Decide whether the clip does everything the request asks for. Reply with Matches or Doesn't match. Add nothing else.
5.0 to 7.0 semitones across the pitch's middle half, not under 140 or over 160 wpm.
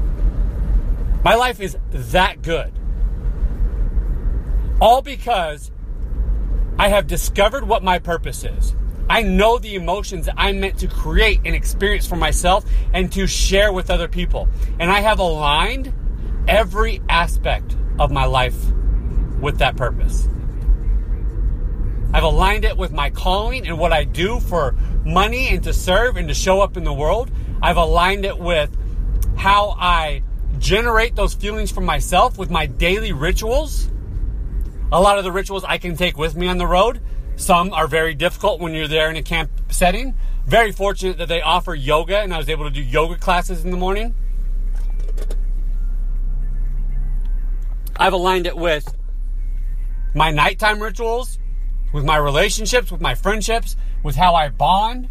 Matches